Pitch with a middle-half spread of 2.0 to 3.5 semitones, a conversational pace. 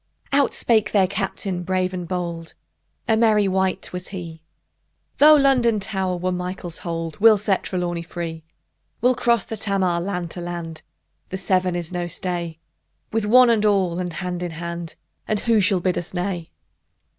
Yes: average, 3.1 semitones; average, 170 wpm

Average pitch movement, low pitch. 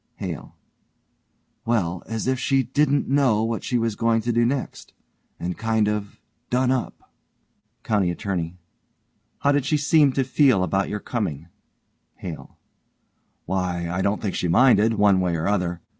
No: wide, 5.7 semitones; low, 110 Hz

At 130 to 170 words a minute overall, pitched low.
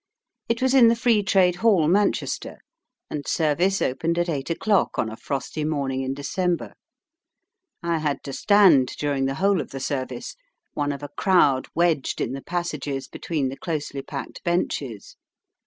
No: average, 165 wpm; medium, 155 Hz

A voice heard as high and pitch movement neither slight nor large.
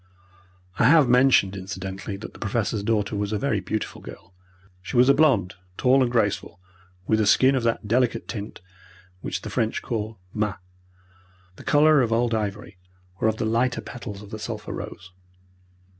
No: low, 110 Hz; average, 3.3 semitones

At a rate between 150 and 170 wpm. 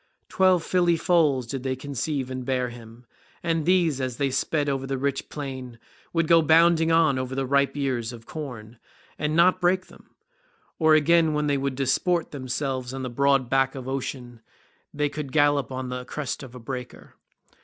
No: average, 185 wpm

